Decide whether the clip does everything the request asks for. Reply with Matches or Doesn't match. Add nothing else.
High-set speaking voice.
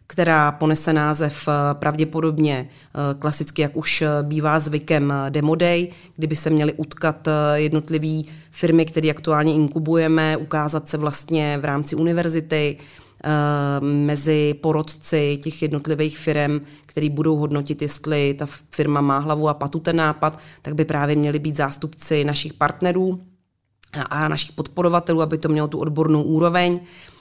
Doesn't match